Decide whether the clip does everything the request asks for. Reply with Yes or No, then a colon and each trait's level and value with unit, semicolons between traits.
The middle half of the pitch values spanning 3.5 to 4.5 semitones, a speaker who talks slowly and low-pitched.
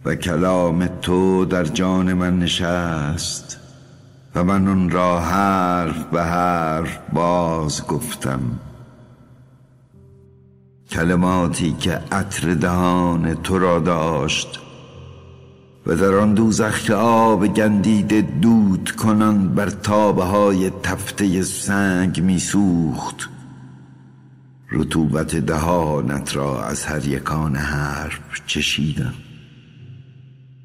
No: average, 5.0 semitones; slow, 90 wpm; very low, 90 Hz